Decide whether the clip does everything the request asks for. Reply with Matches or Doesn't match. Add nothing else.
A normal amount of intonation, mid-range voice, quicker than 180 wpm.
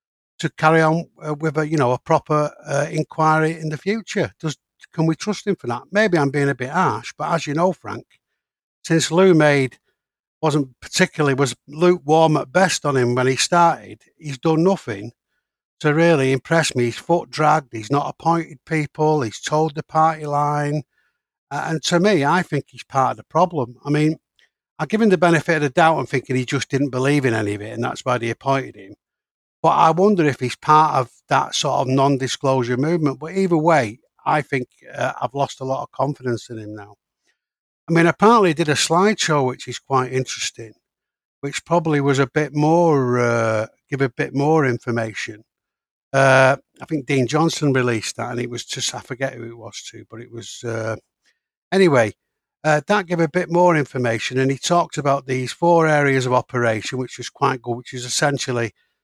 Matches